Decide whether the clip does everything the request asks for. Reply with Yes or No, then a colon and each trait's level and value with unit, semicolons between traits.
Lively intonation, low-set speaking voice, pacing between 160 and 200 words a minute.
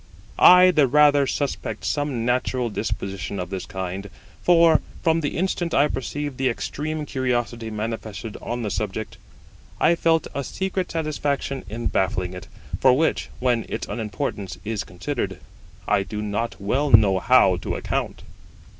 No: wide, 6.0 semitones; low, 125 Hz; average, 145 wpm